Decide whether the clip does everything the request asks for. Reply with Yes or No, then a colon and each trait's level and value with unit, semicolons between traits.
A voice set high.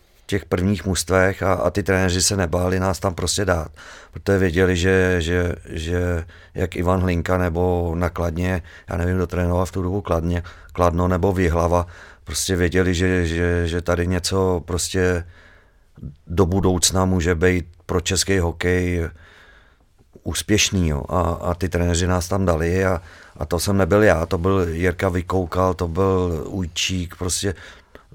No: very low, 90 Hz